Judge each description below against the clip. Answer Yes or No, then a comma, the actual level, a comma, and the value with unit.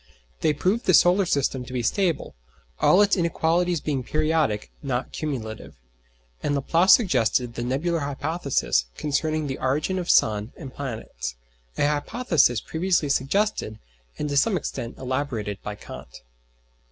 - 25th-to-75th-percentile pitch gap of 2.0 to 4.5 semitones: No, average, 5.3 semitones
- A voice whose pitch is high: No, medium, 145 Hz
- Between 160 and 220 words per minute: No, average, 140 wpm